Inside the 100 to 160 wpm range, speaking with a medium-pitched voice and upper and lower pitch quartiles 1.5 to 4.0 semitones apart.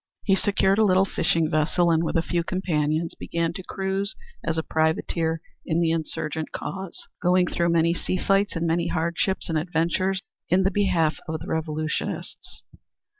No: average, 170 wpm; medium, 170 Hz; narrow, 2.6 semitones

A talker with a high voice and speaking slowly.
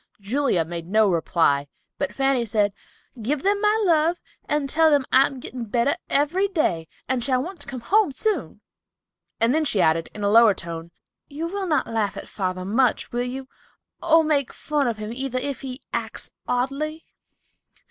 No: very high, 260 Hz; average, 180 wpm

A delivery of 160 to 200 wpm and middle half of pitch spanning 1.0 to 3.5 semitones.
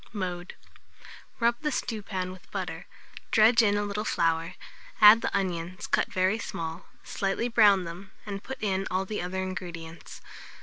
No: average, 150 wpm; average, 2.9 semitones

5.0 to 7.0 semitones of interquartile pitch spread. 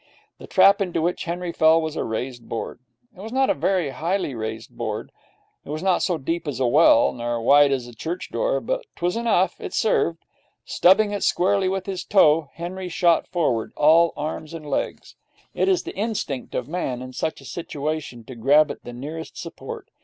Yes: average, 5.3 semitones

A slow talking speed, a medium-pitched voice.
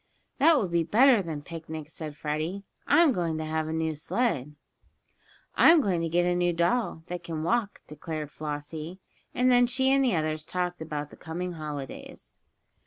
No: average, 175 wpm; medium, 165 Hz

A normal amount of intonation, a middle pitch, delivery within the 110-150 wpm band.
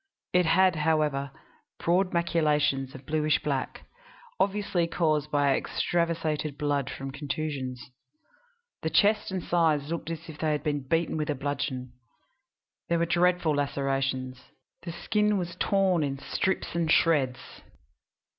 Yes: average, 3.3 semitones; medium, 155 Hz; slow, 135 wpm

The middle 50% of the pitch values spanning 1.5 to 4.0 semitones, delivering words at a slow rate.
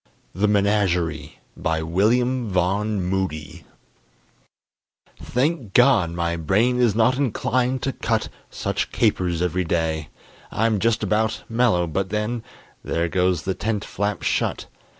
No: average, 4.7 semitones; slow, 125 wpm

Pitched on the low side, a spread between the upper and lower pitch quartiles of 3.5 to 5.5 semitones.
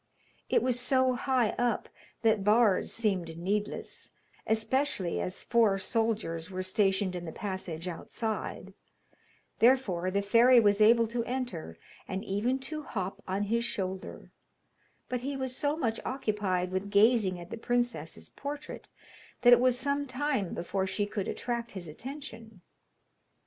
No: high, 220 Hz; average, 4.5 semitones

